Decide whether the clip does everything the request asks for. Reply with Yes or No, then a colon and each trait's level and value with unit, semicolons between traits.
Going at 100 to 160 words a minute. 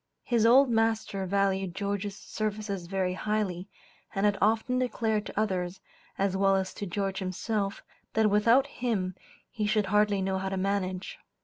Yes: average, 155 wpm